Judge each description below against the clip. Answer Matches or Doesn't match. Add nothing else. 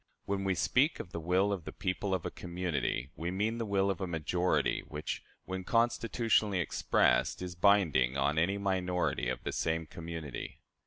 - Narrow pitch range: Doesn't match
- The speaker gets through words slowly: Doesn't match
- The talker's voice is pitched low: Matches